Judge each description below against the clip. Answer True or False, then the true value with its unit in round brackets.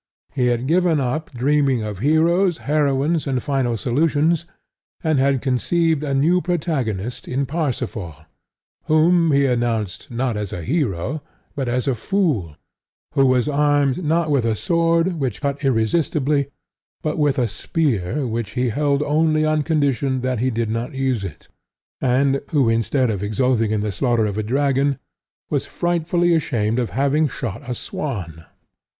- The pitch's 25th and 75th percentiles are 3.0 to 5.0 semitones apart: True (4.6 semitones)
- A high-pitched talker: False (135 Hz)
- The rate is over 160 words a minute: False (155 wpm)